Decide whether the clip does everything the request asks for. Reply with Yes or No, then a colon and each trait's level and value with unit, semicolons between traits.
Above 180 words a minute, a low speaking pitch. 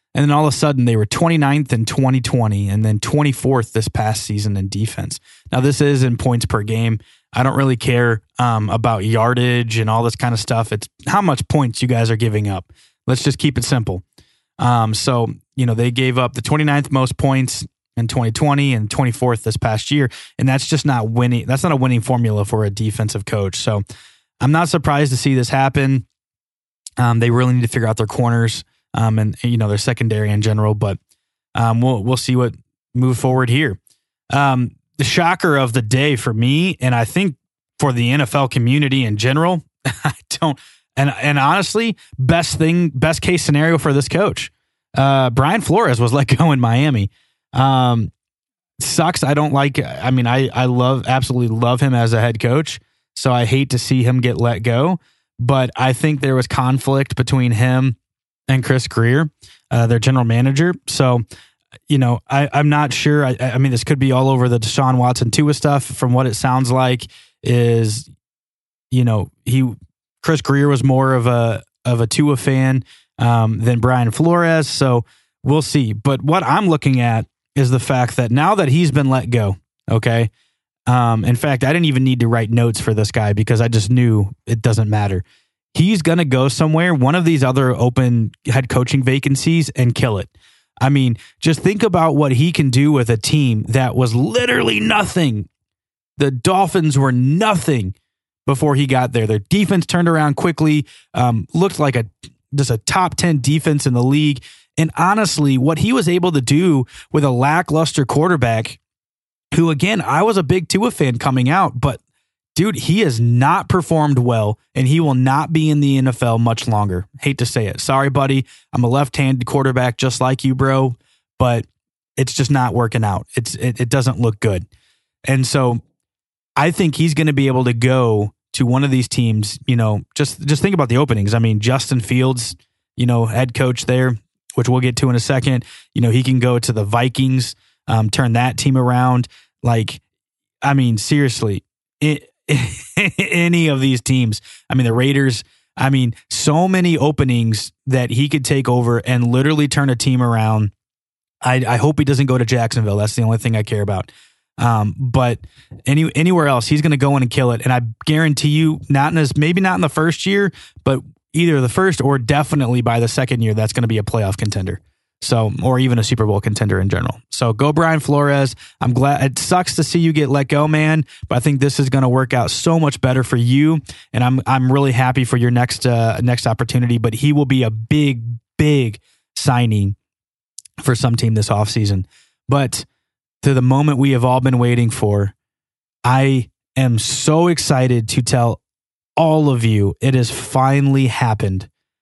Yes: average, 195 wpm; low, 130 Hz